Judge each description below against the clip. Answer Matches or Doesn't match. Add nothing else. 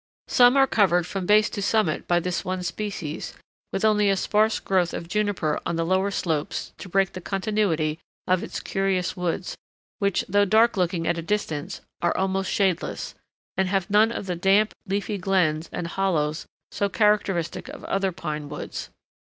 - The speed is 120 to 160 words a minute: Doesn't match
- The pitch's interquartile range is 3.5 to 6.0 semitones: Doesn't match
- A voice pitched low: Doesn't match